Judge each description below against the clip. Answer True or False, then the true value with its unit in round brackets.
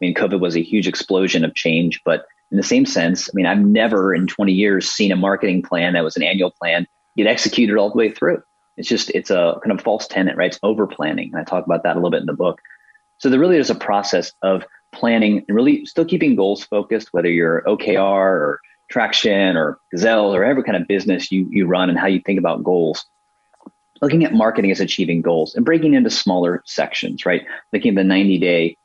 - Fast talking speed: True (230 wpm)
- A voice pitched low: True (100 Hz)